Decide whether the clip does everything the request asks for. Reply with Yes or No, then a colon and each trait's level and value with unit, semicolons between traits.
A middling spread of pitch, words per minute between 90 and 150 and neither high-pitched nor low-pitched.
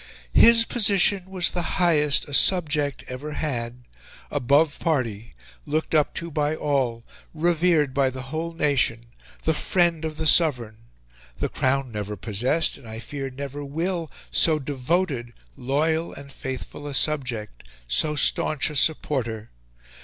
Yes: average, 4.0 semitones; average, 140 wpm; medium, 145 Hz